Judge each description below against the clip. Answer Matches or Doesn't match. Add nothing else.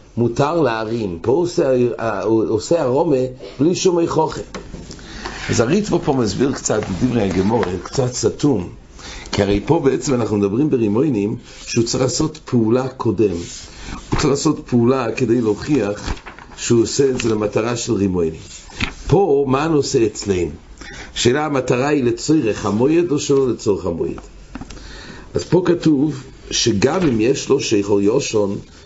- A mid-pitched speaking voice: Doesn't match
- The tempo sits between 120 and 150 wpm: Matches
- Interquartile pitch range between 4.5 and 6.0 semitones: Matches